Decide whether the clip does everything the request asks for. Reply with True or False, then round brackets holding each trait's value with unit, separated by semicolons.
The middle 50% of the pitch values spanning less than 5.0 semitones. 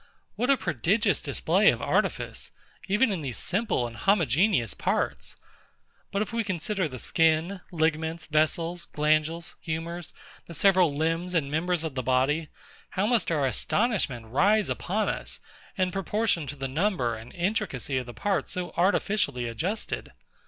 False (5.3 semitones)